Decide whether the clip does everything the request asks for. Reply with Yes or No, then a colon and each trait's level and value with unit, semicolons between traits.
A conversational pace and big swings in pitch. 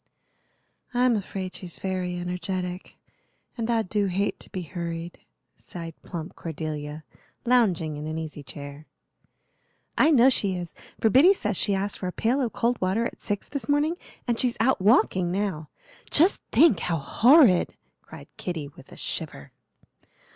Yes: average, 155 wpm; wide, 5.8 semitones